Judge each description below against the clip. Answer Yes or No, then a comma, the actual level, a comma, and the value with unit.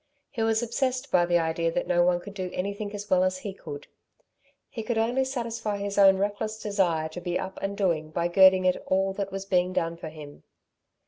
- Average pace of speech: No, fast, 215 wpm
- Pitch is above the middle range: Yes, high, 195 Hz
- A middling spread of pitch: Yes, average, 3.5 semitones